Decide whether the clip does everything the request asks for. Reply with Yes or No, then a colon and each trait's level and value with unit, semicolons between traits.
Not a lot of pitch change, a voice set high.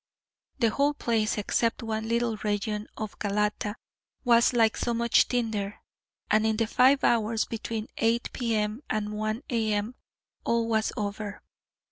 Yes: narrow, 1.7 semitones; high, 220 Hz